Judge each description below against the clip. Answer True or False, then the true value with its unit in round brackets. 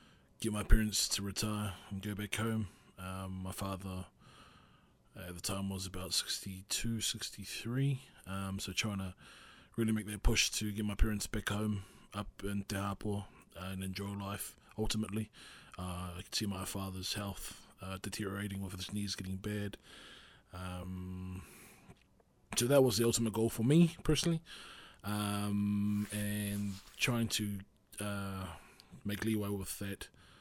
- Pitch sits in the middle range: False (100 Hz)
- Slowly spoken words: False (145 wpm)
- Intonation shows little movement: True (2.0 semitones)